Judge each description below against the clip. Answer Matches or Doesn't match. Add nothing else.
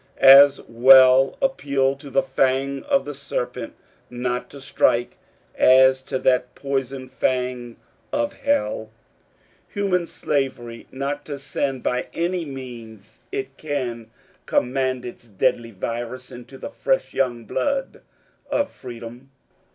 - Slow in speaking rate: Matches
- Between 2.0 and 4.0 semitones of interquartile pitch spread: Matches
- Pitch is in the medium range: Doesn't match